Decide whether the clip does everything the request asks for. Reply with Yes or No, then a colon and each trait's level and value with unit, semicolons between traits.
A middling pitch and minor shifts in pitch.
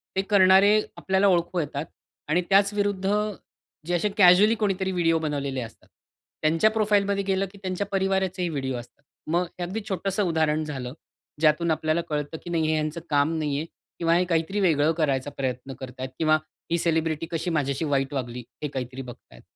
No: medium, 165 Hz; average, 4.7 semitones